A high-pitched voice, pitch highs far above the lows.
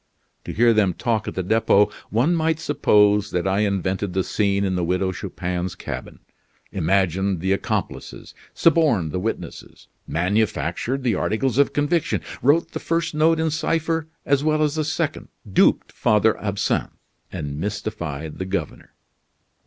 No: low, 105 Hz; wide, 7.7 semitones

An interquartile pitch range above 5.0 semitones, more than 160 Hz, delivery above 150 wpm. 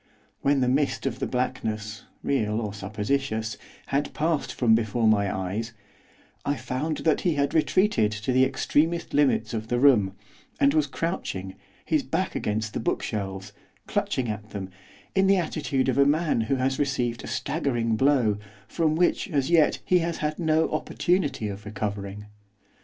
No: wide, 5.5 semitones; low, 130 Hz; average, 165 wpm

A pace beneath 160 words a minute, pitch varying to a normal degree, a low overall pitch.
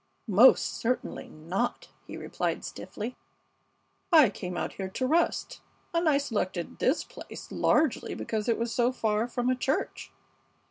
No: average, 145 wpm; average, 3.9 semitones; high, 240 Hz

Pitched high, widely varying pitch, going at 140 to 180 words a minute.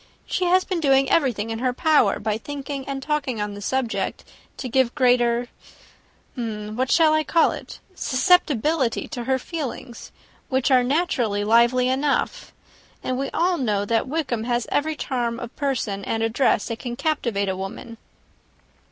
No: very high, 255 Hz; average, 4.0 semitones; average, 160 wpm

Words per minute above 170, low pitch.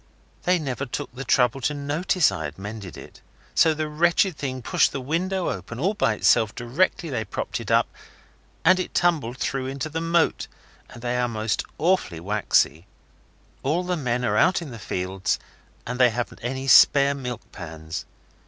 Yes: average, 180 wpm; low, 130 Hz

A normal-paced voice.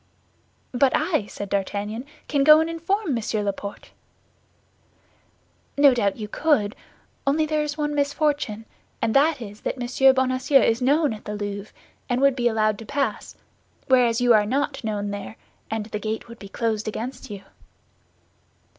Yes: average, 160 wpm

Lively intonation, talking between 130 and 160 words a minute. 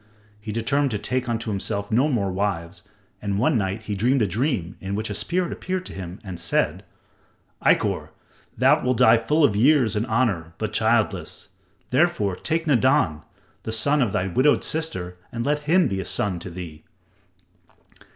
No: wide, 6.3 semitones; average, 175 wpm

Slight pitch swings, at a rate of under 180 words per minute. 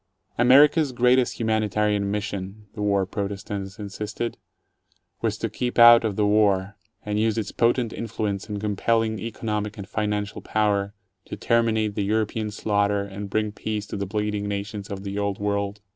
Yes: narrow, 1.4 semitones; average, 160 wpm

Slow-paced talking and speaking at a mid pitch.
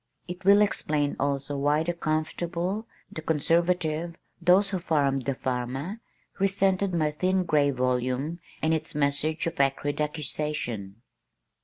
Yes: slow, 130 wpm; medium, 155 Hz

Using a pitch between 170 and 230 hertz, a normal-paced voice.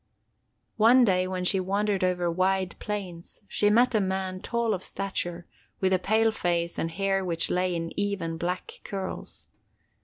Yes: high, 190 Hz; average, 160 wpm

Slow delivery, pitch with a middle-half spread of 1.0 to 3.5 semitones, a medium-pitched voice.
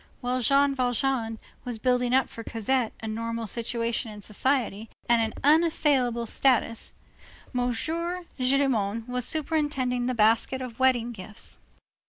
No: slow, 130 wpm; average, 2.7 semitones; high, 245 Hz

